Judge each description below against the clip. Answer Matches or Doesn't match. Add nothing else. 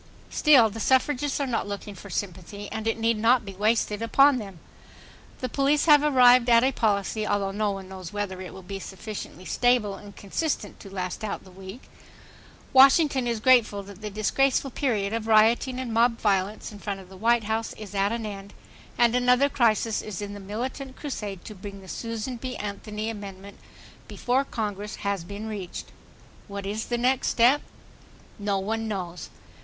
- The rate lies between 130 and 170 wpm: Doesn't match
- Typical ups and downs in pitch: Matches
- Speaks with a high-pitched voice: Matches